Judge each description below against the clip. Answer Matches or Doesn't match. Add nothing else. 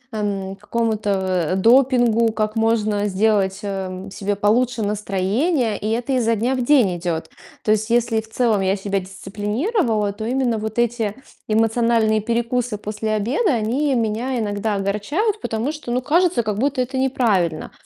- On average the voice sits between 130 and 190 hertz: Doesn't match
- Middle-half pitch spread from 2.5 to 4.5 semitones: Matches